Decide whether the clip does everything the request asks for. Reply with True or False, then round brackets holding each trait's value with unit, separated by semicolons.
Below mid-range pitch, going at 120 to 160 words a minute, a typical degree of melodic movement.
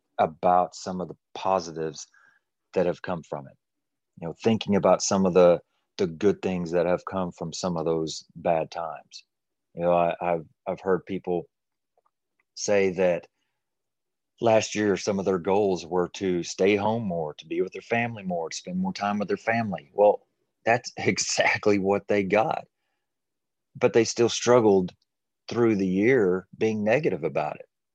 False (95 Hz; 170 wpm; 3.1 semitones)